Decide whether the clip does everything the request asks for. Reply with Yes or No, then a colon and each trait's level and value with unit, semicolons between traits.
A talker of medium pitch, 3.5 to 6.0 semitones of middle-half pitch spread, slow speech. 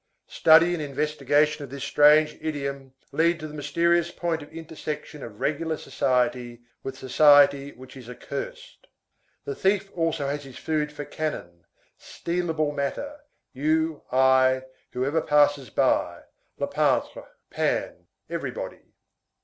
No: medium, 150 Hz; average, 3.0 semitones; slow, 125 wpm